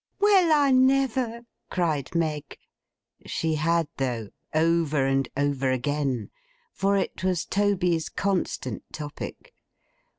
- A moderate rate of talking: No, slow, 100 wpm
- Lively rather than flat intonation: Yes, wide, 6.1 semitones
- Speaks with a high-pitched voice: No, medium, 165 Hz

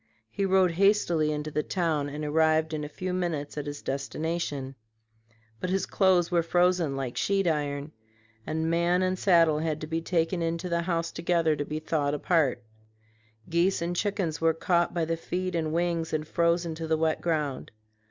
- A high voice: No, medium, 165 Hz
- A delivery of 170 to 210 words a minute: Yes, average, 180 wpm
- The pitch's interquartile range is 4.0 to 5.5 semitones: No, narrow, 2.4 semitones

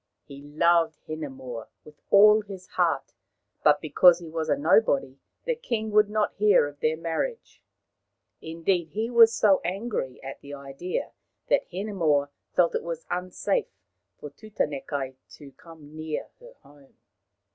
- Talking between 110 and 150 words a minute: Yes, average, 145 wpm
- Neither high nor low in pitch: Yes, medium, 165 Hz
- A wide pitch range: Yes, wide, 6.3 semitones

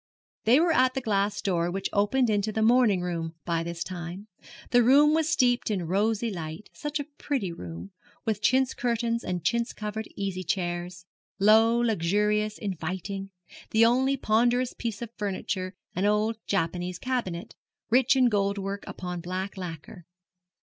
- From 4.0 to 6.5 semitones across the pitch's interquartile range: Yes, average, 4.6 semitones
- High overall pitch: Yes, high, 205 Hz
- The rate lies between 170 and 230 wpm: No, average, 155 wpm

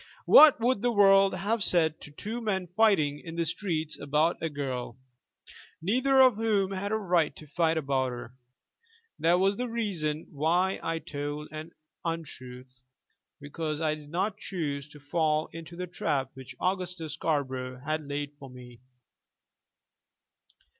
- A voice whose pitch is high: No, medium, 160 Hz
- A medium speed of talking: Yes, average, 150 wpm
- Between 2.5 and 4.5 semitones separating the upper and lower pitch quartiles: No, average, 4.9 semitones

